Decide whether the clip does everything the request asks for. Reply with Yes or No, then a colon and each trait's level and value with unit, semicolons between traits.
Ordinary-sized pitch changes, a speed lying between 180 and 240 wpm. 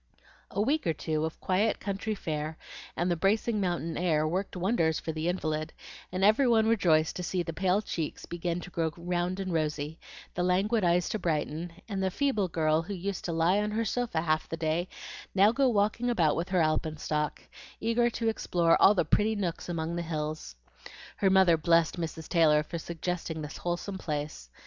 Yes: average, 3.8 semitones; average, 190 wpm